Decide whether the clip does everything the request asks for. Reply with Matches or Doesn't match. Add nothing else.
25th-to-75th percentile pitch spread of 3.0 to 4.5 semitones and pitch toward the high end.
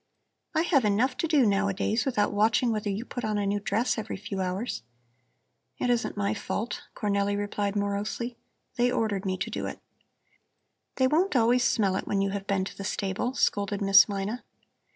Matches